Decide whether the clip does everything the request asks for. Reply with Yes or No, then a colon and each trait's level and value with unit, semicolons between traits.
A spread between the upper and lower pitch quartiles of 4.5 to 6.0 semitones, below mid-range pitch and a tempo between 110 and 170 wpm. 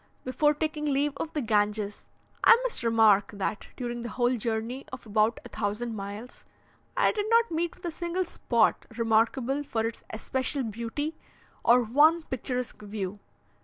No: average, 5.2 semitones; high, 240 Hz; average, 160 wpm